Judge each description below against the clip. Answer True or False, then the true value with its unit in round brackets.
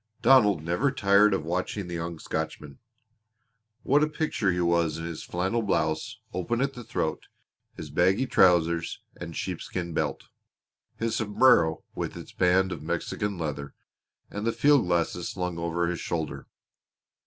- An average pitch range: True (3.8 semitones)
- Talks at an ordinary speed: True (150 wpm)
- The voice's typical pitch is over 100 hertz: False (90 Hz)